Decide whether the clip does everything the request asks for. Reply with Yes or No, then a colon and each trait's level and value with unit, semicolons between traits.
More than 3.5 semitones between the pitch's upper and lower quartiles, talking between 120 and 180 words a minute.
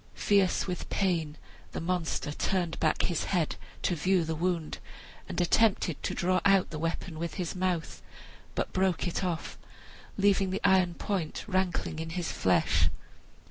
No: narrow, 2.5 semitones; average, 155 wpm